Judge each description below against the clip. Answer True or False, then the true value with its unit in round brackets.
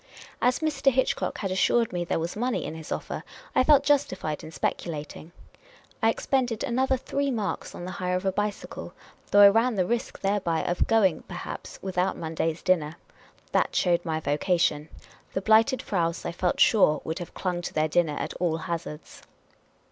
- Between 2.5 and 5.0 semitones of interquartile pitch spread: False (5.4 semitones)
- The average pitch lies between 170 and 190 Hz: True (185 Hz)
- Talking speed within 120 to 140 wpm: False (180 wpm)